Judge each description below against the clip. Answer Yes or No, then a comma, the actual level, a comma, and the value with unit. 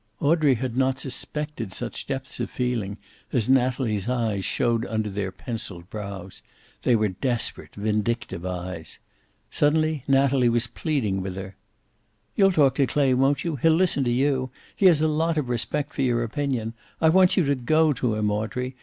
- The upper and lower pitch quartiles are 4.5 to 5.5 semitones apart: Yes, average, 5.0 semitones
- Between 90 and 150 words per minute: No, average, 170 wpm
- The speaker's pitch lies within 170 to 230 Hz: No, low, 125 Hz